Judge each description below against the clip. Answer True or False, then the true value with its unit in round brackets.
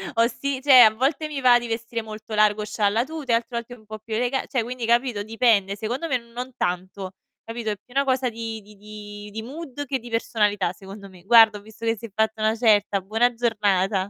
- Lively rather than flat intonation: False (2.7 semitones)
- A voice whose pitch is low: False (225 Hz)